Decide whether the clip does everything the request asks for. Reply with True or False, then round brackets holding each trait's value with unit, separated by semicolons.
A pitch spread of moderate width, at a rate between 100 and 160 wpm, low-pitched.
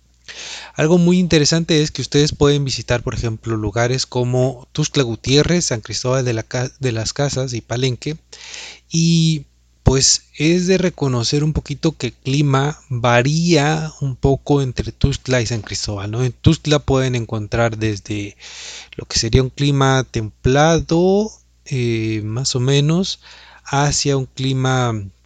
True (4.2 semitones; 145 wpm; 130 Hz)